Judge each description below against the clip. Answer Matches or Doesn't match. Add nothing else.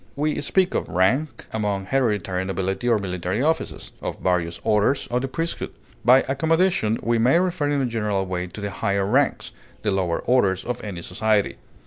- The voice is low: Matches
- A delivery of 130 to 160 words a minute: Doesn't match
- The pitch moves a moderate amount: Doesn't match